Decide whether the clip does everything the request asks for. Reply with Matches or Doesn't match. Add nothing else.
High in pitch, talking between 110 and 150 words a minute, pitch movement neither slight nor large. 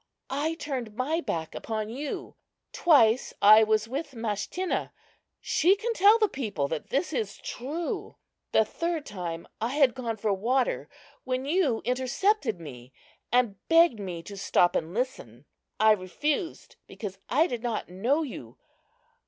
Doesn't match